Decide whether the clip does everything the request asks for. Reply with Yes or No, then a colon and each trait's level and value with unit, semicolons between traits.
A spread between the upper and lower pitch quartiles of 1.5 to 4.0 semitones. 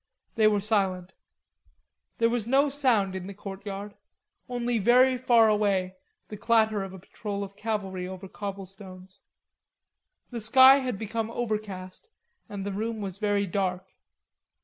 Yes: average, 3.0 semitones